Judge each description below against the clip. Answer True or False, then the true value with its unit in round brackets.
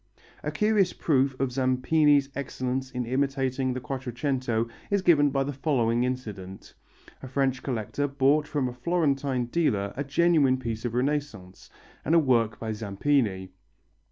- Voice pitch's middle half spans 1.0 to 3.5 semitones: True (2.9 semitones)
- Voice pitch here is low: True (130 Hz)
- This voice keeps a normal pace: True (145 wpm)